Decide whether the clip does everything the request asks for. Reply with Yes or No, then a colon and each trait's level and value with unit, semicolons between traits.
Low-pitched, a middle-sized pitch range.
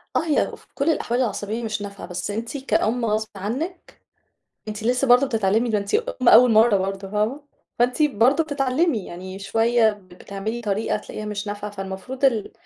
No: high, 220 Hz; average, 3.7 semitones